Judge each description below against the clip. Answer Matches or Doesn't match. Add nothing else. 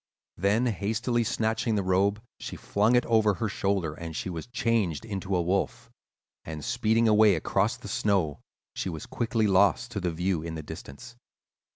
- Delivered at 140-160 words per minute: Doesn't match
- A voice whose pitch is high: Doesn't match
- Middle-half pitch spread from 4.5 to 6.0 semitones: Doesn't match